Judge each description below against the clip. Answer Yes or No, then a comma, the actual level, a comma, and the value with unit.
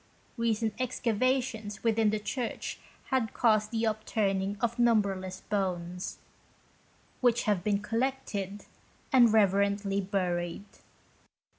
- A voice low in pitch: No, high, 210 Hz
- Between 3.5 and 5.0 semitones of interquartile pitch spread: No, average, 2.8 semitones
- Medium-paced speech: No, slow, 100 wpm